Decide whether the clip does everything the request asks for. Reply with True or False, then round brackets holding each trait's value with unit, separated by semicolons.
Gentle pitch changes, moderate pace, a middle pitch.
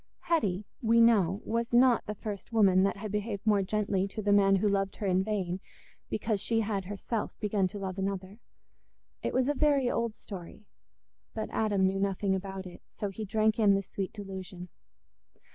False (2.2 semitones; 185 wpm; 200 Hz)